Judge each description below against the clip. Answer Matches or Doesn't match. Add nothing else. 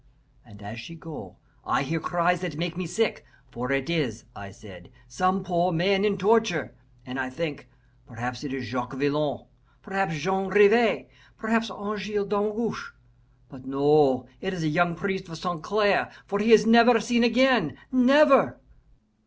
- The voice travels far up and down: Matches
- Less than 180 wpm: Matches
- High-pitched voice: Doesn't match